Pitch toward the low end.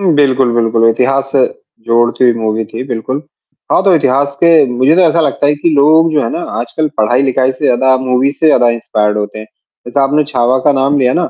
Yes: low, 130 Hz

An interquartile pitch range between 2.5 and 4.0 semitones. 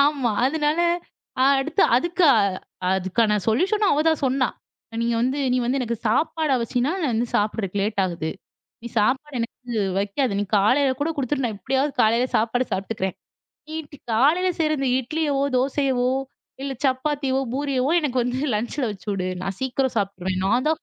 No: average, 4.5 semitones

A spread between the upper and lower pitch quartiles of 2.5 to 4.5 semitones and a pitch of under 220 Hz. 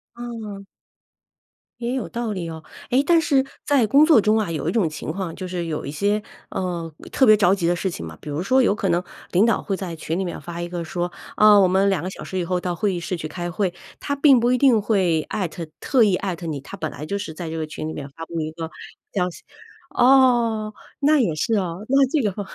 No: average, 5.1 semitones; high, 190 Hz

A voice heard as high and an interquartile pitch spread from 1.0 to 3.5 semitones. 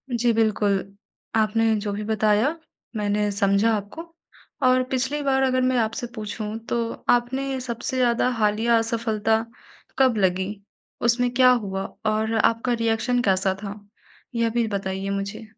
Yes: high, 225 Hz; average, 2.8 semitones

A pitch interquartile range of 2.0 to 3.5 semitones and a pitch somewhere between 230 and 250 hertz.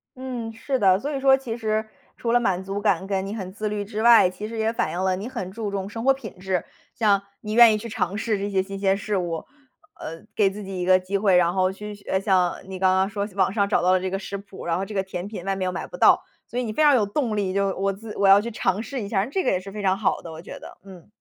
No: average, 2.7 semitones; high, 200 Hz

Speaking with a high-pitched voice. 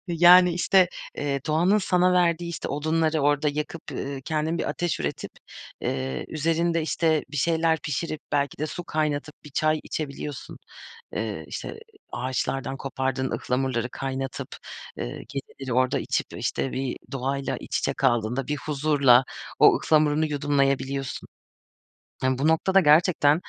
No: medium, 150 Hz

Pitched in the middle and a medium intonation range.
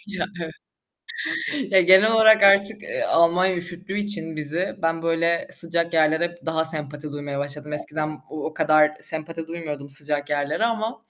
Yes: medium, 165 Hz; average, 3.7 semitones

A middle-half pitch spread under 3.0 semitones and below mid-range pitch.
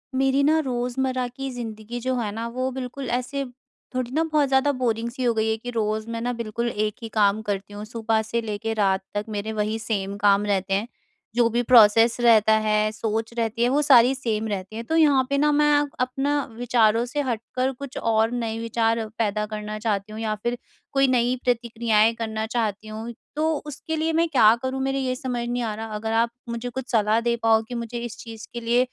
No: narrow, 2.6 semitones; high, 230 Hz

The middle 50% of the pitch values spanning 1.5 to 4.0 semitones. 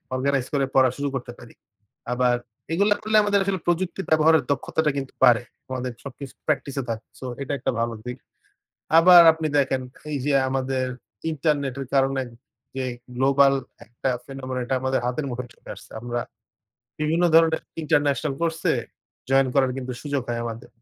Yes: average, 3.2 semitones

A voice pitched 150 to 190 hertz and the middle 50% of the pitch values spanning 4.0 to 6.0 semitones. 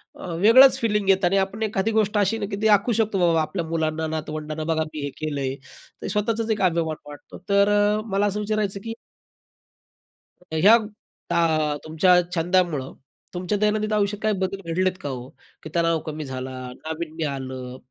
Yes: medium, 185 Hz; average, 4.9 semitones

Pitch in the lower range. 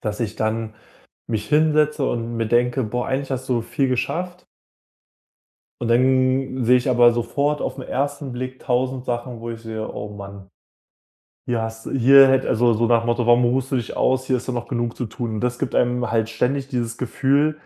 Yes: low, 125 Hz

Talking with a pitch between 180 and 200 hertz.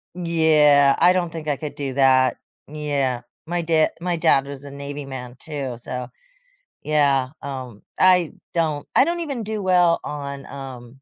No: medium, 145 Hz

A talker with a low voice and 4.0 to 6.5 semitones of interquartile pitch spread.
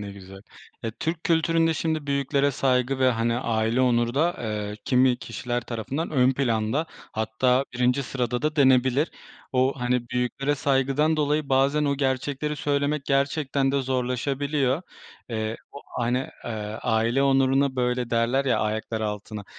No: low, 130 Hz; average, 2.9 semitones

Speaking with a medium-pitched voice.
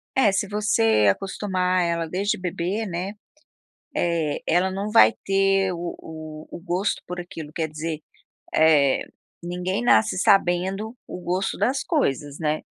Yes: medium, 180 Hz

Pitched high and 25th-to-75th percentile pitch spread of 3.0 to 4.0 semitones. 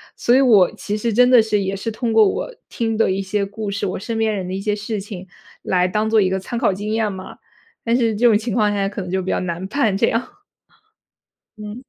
No: high, 210 Hz; narrow, 2.6 semitones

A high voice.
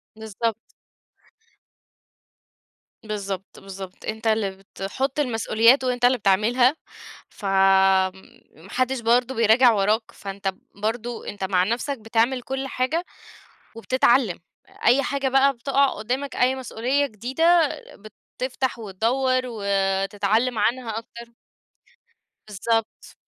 Yes: high, 230 Hz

